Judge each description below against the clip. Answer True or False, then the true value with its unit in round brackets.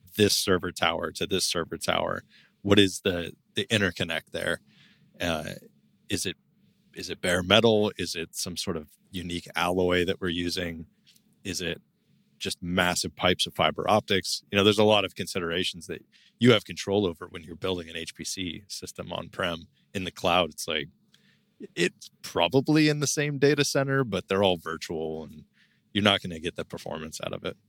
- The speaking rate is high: False (185 wpm)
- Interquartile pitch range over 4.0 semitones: False (3.3 semitones)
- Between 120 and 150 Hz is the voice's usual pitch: False (95 Hz)